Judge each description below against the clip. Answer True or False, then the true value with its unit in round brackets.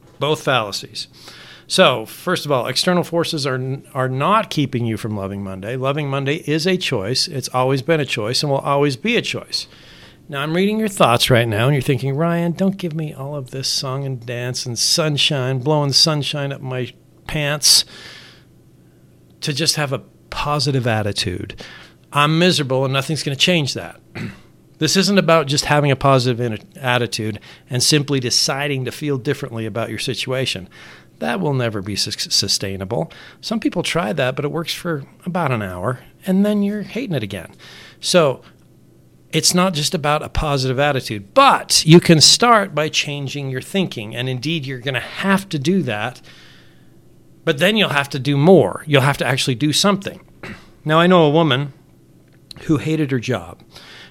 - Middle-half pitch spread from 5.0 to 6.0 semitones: False (4.0 semitones)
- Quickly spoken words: False (175 wpm)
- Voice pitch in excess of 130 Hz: True (140 Hz)